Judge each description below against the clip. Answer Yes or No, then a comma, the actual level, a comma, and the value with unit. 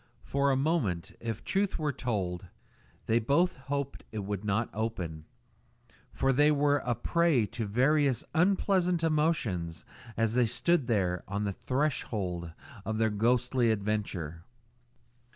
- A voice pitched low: Yes, low, 120 Hz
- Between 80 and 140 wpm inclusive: Yes, slow, 135 wpm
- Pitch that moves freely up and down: Yes, wide, 6.0 semitones